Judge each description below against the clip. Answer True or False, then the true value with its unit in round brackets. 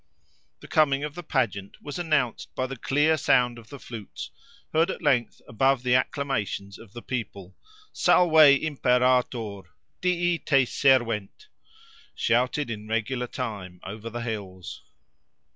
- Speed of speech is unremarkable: False (125 wpm)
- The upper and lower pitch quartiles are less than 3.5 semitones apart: False (4.9 semitones)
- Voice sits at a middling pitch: False (125 Hz)